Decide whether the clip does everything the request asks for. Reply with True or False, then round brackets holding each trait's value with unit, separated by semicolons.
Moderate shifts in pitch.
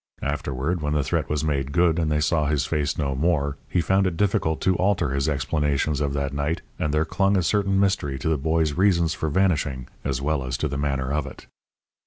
True (3.2 semitones)